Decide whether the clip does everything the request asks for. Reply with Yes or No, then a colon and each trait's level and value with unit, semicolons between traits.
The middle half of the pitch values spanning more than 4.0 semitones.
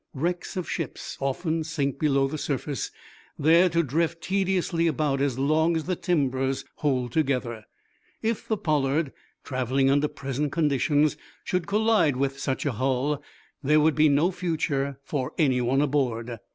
No: average, 3.4 semitones